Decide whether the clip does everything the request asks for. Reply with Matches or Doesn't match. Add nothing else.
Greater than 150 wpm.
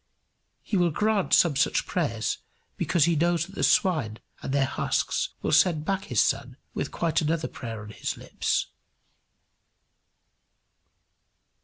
Doesn't match